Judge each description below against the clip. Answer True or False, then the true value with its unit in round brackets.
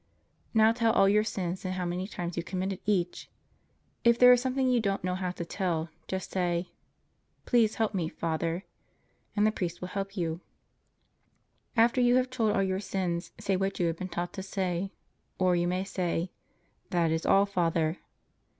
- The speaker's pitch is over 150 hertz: True (185 Hz)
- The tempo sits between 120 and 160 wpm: False (185 wpm)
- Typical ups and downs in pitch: True (3.1 semitones)